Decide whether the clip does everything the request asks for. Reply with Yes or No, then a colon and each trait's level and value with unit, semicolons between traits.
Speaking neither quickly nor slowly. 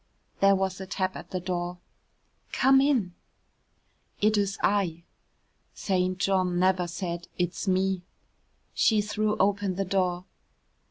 No: slow, 120 wpm